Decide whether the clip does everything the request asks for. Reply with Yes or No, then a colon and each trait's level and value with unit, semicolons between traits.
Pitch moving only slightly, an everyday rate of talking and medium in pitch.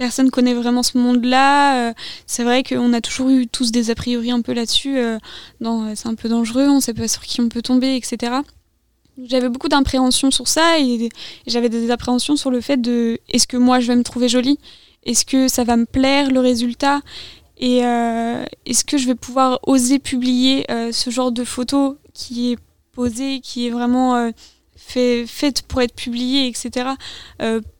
No: narrow, 1.6 semitones; average, 200 wpm; very high, 250 Hz